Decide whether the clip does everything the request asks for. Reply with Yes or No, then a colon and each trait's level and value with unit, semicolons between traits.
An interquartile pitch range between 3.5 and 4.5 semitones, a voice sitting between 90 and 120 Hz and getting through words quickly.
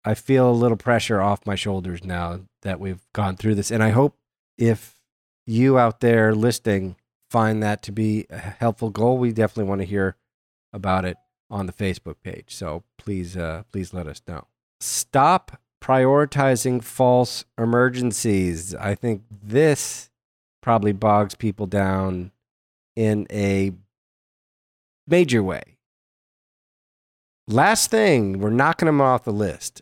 No: average, 3.9 semitones; low, 105 Hz; average, 140 wpm